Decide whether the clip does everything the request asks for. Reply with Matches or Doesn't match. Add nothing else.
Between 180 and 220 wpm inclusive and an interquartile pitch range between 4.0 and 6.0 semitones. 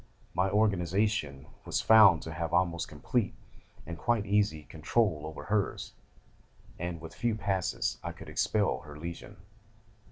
Doesn't match